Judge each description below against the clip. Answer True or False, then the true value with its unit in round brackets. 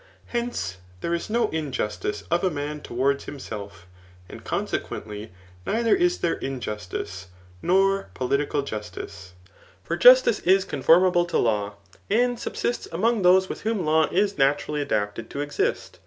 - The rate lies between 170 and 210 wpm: False (140 wpm)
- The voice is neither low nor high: True (150 Hz)